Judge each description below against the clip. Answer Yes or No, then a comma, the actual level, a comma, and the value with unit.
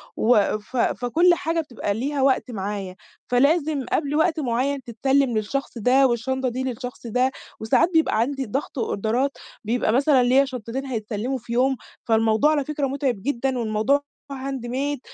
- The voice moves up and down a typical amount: Yes, average, 3.2 semitones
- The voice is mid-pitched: No, very high, 255 Hz